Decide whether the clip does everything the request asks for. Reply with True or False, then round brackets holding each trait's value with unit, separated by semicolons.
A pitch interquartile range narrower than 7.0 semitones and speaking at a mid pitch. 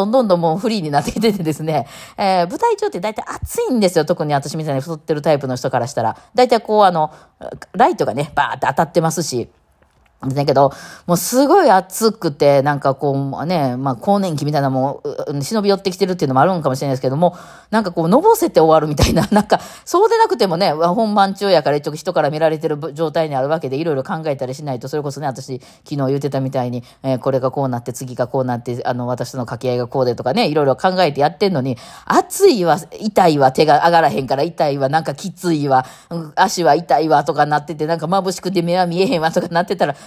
True (5.6 semitones; 155 Hz)